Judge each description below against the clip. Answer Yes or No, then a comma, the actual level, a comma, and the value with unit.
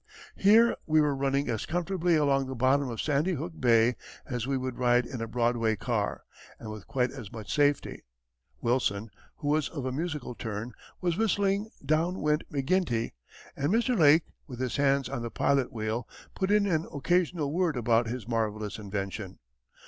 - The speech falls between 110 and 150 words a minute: No, average, 175 wpm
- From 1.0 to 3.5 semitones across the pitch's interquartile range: No, wide, 5.4 semitones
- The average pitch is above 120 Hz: Yes, low, 135 Hz